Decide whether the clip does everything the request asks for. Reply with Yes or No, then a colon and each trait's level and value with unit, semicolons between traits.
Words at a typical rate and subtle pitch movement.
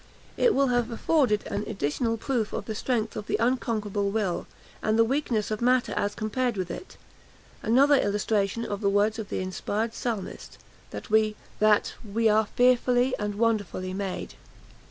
No: average, 155 wpm; average, 3.0 semitones